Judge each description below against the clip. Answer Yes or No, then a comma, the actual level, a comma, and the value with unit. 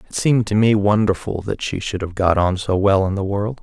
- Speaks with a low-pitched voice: Yes, low, 100 Hz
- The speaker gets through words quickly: Yes, fast, 265 wpm